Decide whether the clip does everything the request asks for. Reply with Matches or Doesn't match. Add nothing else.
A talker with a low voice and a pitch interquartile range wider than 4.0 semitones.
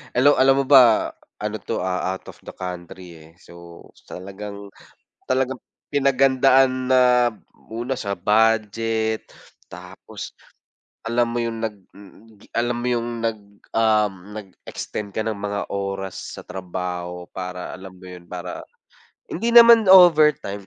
Matches